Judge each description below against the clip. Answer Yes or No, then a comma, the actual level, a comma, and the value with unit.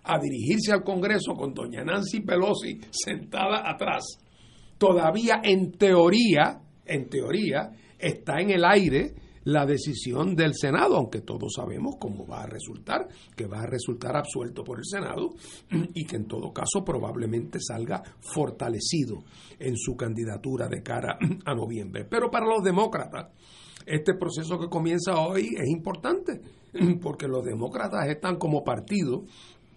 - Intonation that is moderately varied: No, wide, 7.1 semitones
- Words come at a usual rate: Yes, average, 140 wpm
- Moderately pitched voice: Yes, medium, 165 Hz